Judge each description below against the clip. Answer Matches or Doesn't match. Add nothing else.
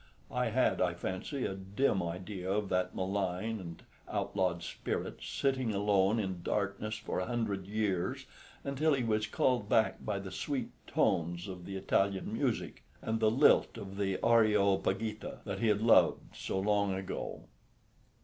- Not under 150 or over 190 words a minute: Matches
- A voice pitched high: Doesn't match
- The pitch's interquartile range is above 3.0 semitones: Doesn't match